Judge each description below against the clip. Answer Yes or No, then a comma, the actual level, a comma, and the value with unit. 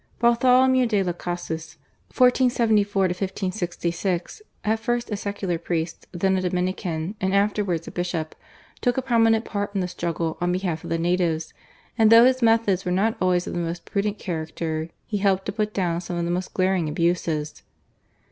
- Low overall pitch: No, medium, 185 Hz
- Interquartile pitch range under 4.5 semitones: Yes, average, 3.7 semitones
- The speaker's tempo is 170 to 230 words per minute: Yes, average, 175 wpm